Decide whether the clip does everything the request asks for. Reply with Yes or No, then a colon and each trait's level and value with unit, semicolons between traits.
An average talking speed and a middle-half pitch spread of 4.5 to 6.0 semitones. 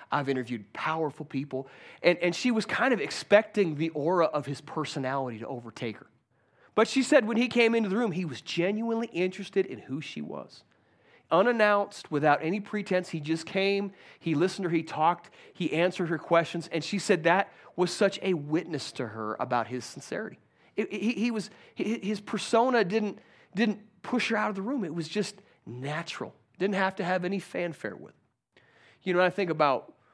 Yes: average, 195 wpm; average, 5.0 semitones